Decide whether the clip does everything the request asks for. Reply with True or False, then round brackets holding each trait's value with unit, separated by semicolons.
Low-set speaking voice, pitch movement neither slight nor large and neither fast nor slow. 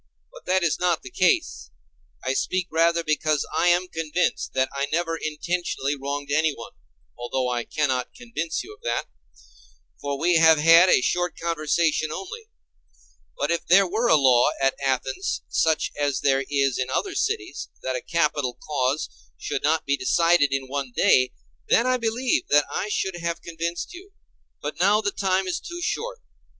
False (155 Hz; 4.7 semitones; 170 wpm)